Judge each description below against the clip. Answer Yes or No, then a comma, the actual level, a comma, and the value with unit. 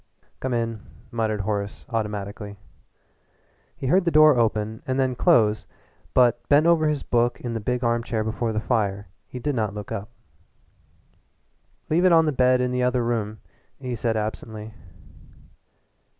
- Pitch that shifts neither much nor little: Yes, average, 3.0 semitones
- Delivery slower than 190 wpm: Yes, average, 155 wpm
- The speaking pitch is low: Yes, low, 115 Hz